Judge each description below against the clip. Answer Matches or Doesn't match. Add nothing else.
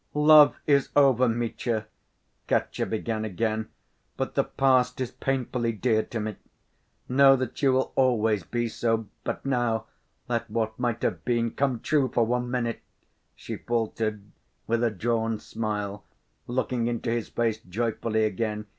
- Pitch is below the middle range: Matches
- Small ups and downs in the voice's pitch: Matches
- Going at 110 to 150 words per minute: Matches